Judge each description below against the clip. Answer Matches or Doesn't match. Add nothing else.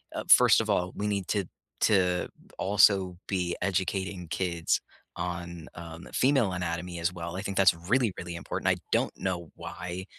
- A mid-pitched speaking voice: Doesn't match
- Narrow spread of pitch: Matches